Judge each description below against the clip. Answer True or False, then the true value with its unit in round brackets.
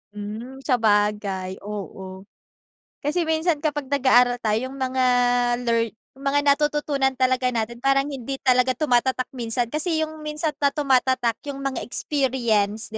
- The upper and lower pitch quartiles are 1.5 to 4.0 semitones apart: True (3.7 semitones)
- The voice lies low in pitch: False (260 Hz)